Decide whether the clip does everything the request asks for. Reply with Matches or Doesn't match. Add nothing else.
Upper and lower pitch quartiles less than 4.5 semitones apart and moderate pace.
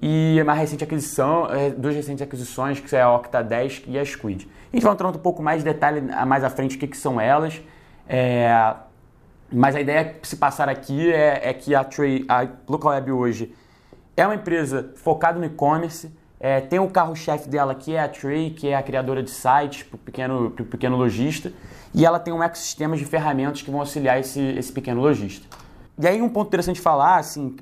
Doesn't match